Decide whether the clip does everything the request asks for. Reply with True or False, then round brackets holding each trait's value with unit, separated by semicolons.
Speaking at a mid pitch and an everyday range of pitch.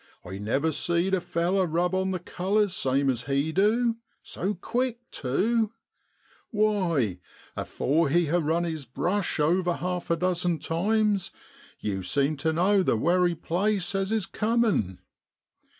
True (175 Hz; 4.6 semitones)